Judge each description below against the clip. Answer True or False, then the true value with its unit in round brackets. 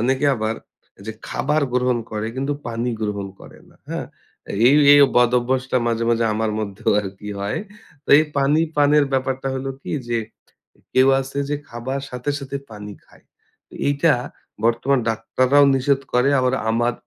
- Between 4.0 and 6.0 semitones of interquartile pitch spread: False (3.2 semitones)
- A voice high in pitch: False (125 Hz)